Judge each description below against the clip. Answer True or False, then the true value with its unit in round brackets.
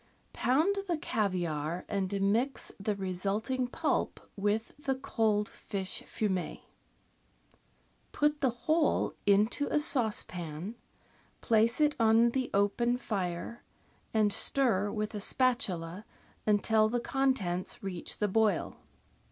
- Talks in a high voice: True (215 Hz)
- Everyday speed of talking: False (120 wpm)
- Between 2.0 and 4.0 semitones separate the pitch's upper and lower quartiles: False (4.4 semitones)